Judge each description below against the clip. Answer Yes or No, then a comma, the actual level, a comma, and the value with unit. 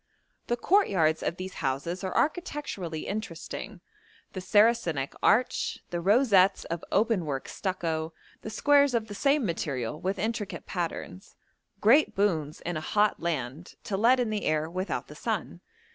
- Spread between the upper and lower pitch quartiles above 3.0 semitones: Yes, average, 5.3 semitones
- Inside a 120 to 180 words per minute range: Yes, average, 150 wpm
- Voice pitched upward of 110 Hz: Yes, high, 190 Hz